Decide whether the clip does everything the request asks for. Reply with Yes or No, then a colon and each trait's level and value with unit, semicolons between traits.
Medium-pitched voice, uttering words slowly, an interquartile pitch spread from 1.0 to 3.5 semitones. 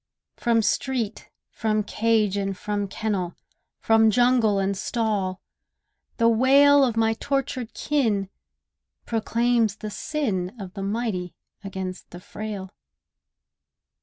No: high, 220 Hz; slow, 110 wpm; average, 3.2 semitones